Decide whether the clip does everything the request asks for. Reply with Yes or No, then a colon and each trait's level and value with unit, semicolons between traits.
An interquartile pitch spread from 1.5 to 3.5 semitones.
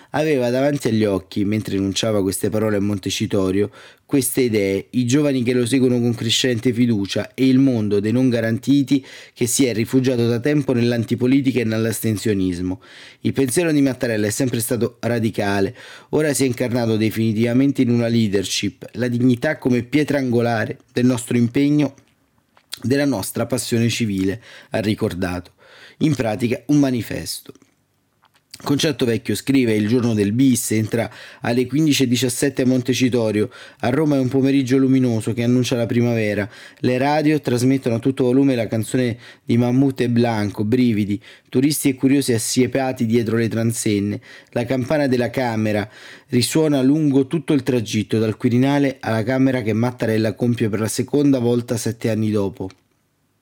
Yes: average, 3.2 semitones